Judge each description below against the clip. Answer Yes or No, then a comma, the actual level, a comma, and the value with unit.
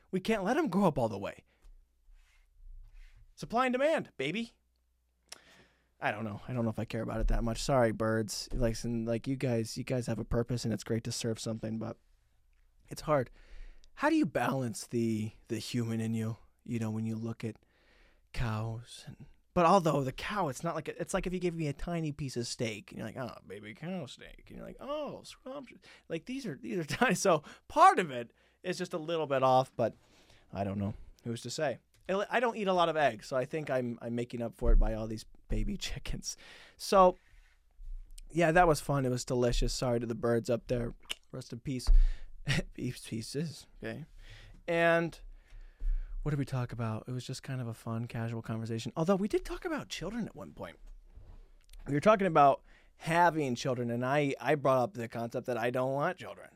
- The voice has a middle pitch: No, low, 125 Hz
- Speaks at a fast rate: Yes, fast, 215 wpm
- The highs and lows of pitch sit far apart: Yes, wide, 6.2 semitones